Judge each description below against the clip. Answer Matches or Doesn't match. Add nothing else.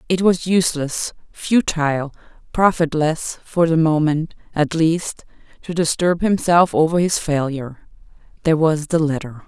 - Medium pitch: Matches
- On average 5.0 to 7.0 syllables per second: Doesn't match